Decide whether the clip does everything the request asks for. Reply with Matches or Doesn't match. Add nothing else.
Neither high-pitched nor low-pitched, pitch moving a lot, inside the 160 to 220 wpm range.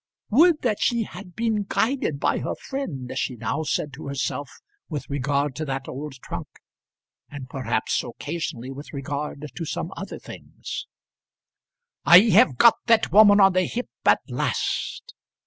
Doesn't match